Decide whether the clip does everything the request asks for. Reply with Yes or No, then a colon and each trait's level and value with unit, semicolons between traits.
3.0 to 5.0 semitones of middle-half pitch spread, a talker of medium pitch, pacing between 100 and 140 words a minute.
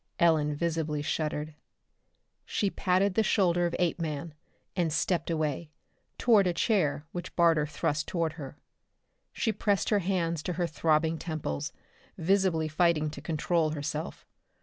No: narrow, 2.6 semitones; medium, 165 Hz; slow, 135 wpm